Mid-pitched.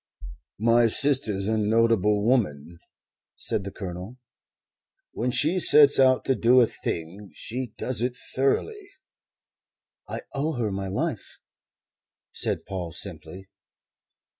No: low, 115 Hz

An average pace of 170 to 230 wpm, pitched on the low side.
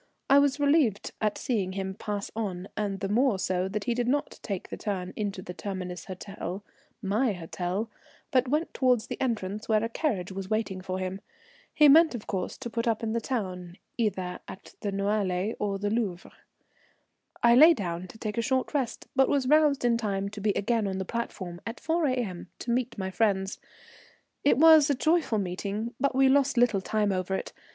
No: average, 200 wpm; high, 210 Hz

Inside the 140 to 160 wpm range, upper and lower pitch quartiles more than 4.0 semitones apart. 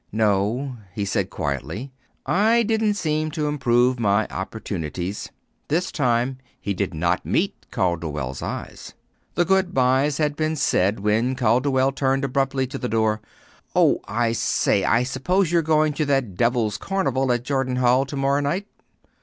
Yes: average, 155 wpm; wide, 5.5 semitones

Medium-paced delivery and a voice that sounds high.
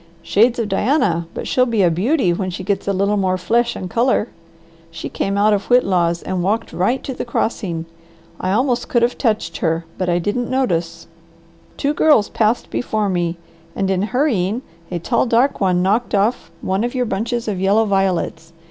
Yes: average, 190 wpm; high, 205 Hz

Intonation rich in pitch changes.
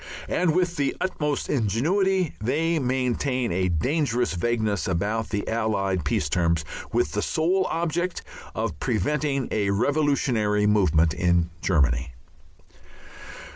Yes: wide, 8.1 semitones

